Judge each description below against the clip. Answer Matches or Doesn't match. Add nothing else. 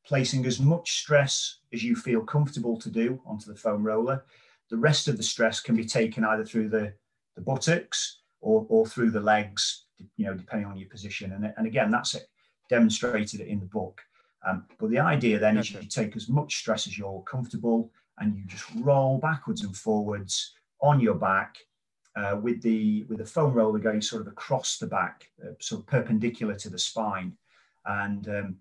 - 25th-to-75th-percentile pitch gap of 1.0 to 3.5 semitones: Doesn't match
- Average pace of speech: Matches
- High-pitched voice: Doesn't match